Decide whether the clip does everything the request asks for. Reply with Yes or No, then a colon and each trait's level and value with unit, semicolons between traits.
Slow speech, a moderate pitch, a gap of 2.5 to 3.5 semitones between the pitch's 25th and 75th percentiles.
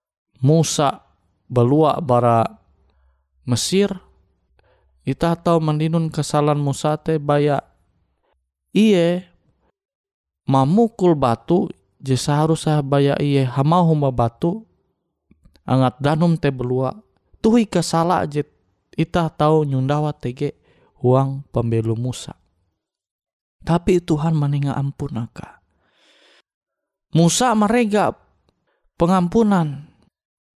No: slow, 80 wpm; medium, 150 Hz; average, 4.8 semitones